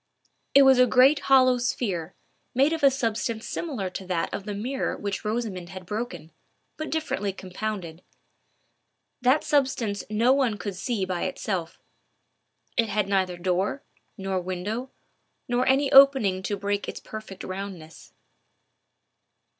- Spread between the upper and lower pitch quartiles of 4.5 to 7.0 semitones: Yes, average, 5.3 semitones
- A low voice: No, high, 210 Hz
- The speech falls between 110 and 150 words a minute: Yes, average, 140 wpm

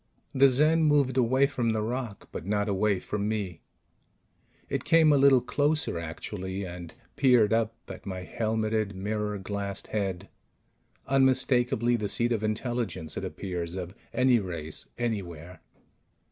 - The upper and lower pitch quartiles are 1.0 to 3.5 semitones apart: No, average, 4.9 semitones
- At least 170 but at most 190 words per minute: No, average, 140 wpm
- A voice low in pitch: Yes, low, 110 Hz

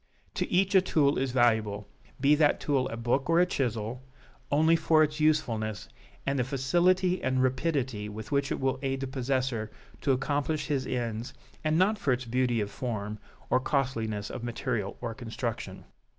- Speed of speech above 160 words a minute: Yes, average, 175 wpm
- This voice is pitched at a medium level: No, low, 130 Hz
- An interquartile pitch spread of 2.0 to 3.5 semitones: No, average, 4.1 semitones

